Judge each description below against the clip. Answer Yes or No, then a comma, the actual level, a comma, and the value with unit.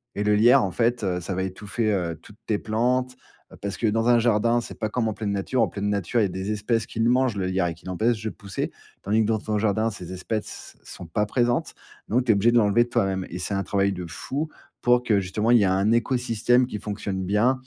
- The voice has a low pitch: Yes, low, 105 Hz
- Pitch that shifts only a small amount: No, average, 3.3 semitones